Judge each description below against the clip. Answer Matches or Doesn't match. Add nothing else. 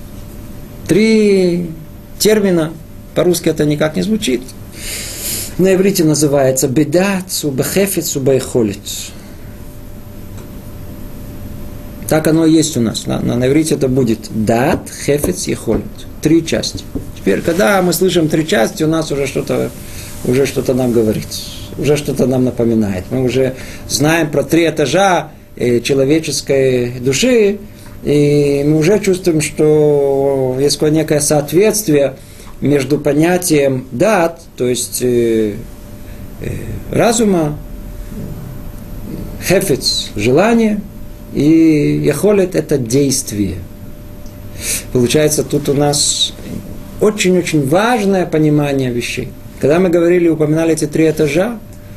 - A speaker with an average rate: Doesn't match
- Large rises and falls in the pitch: Matches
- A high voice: Doesn't match